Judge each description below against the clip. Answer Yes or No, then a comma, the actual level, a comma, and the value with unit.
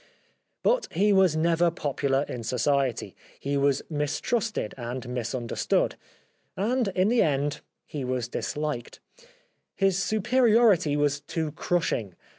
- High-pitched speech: No, medium, 150 Hz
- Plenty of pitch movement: Yes, wide, 6.2 semitones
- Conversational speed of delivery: No, slow, 95 wpm